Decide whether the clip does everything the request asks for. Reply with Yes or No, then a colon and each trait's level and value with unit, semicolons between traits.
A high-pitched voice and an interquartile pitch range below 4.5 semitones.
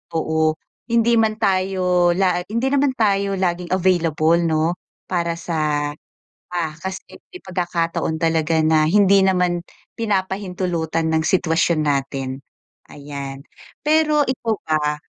No: medium, 175 Hz; average, 3.6 semitones